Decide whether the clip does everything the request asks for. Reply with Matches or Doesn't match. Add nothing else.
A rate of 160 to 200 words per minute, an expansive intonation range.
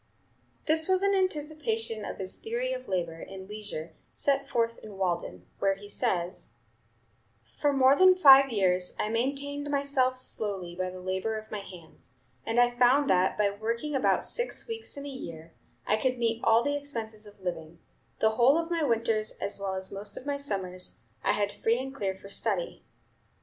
Matches